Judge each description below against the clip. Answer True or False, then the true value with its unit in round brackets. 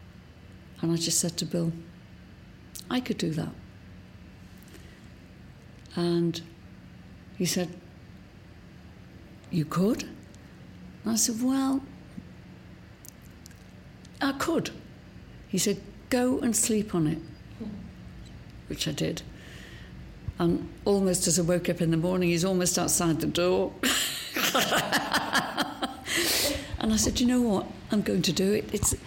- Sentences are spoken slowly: True (120 wpm)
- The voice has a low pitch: False (175 Hz)